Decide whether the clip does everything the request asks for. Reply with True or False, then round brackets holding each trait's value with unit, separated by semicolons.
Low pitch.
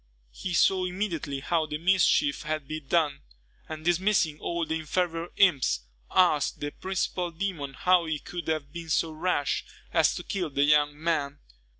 False (160 Hz)